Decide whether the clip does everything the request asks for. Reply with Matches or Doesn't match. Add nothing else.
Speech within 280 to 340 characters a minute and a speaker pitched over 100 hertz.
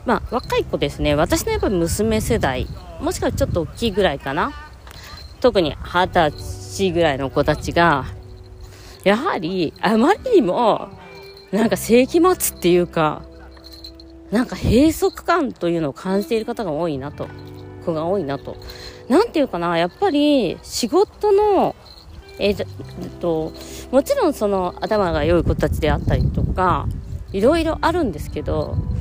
Matches